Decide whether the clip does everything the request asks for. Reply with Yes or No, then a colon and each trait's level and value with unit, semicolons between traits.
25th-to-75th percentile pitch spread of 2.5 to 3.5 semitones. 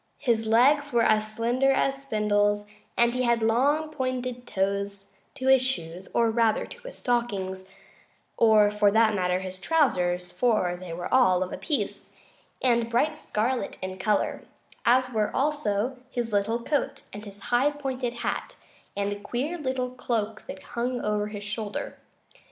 No: average, 3.9 semitones